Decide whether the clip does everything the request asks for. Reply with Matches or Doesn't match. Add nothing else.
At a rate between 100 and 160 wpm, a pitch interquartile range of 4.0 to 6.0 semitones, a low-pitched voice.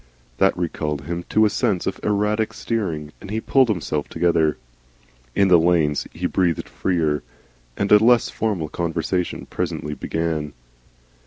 Matches